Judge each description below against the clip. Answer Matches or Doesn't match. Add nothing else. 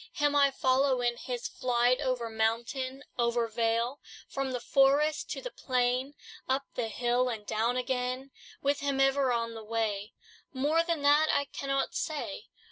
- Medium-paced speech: Matches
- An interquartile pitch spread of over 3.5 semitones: Doesn't match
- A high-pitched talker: Matches